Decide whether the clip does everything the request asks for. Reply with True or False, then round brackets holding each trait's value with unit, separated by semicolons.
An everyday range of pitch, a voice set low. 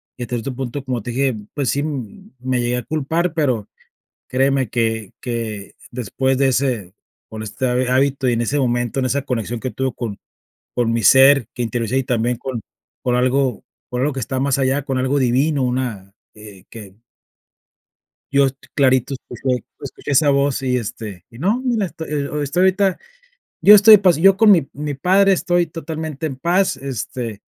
True (3.1 semitones; 130 Hz)